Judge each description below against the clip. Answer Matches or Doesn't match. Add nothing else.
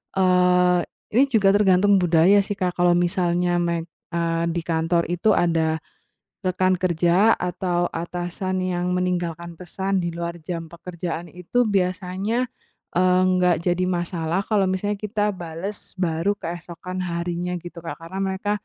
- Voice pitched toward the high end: Doesn't match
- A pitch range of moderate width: Doesn't match